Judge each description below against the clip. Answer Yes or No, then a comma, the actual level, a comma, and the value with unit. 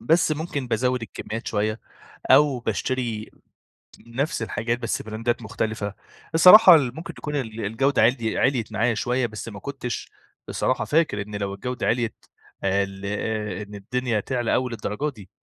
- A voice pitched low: Yes, low, 115 Hz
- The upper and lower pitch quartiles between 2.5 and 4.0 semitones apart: Yes, average, 3.3 semitones